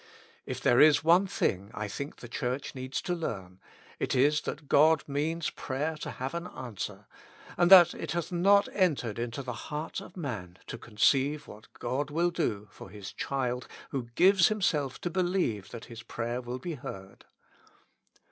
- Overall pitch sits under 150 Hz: Yes, medium, 140 Hz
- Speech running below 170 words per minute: No, average, 175 wpm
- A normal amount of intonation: No, wide, 6.0 semitones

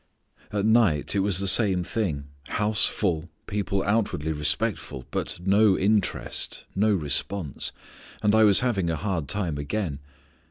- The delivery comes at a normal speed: Yes, average, 145 wpm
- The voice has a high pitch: No, low, 100 Hz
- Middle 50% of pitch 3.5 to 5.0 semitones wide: Yes, average, 4.3 semitones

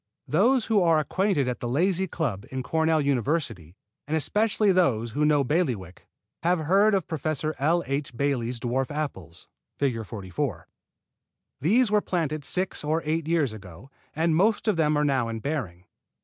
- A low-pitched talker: No, medium, 150 Hz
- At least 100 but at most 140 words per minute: No, average, 165 wpm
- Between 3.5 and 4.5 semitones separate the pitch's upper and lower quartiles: No, wide, 5.4 semitones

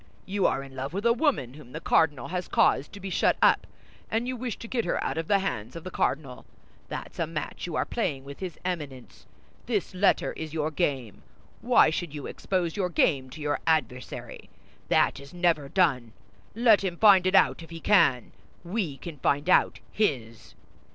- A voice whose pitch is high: No, medium, 165 Hz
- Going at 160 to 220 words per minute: Yes, average, 200 wpm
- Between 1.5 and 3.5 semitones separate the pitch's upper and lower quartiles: No, wide, 5.6 semitones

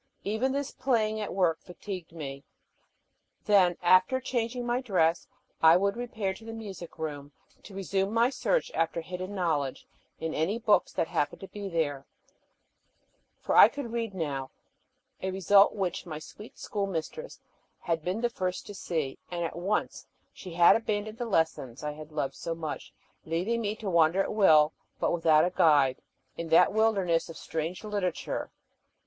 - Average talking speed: Yes, average, 165 wpm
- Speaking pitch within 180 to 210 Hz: Yes, medium, 185 Hz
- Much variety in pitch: No, average, 4.8 semitones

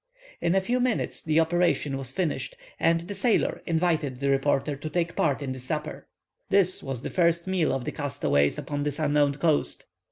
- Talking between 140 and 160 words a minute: No, average, 190 wpm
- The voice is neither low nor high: Yes, medium, 155 Hz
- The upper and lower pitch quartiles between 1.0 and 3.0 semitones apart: No, average, 3.7 semitones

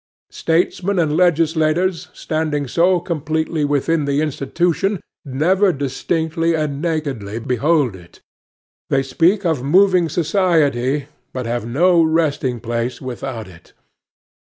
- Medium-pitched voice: Yes, medium, 155 Hz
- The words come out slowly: Yes, slow, 110 wpm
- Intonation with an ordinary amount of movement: Yes, average, 4.1 semitones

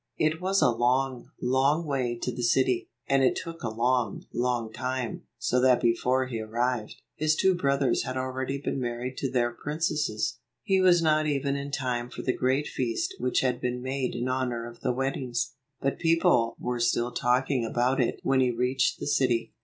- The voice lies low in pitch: Yes, low, 130 Hz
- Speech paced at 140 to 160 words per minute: No, average, 195 wpm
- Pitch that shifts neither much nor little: No, narrow, 2.3 semitones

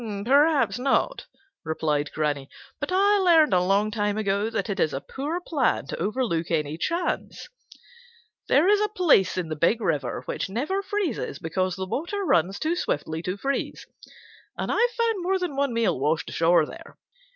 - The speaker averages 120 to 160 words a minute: No, average, 175 wpm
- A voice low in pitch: No, high, 220 Hz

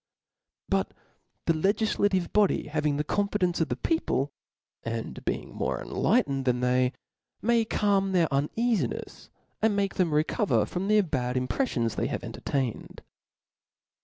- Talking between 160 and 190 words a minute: No, slow, 135 wpm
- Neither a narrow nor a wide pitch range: No, wide, 7.0 semitones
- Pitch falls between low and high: Yes, medium, 170 Hz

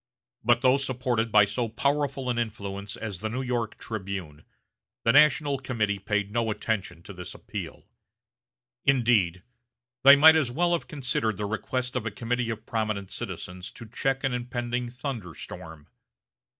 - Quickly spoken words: No, average, 155 wpm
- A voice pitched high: No, low, 115 Hz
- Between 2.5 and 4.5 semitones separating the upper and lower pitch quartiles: Yes, average, 3.8 semitones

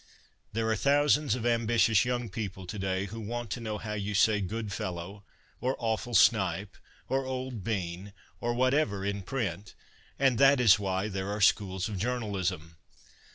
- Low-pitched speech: Yes, low, 105 Hz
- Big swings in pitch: No, average, 3.7 semitones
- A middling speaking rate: Yes, average, 165 wpm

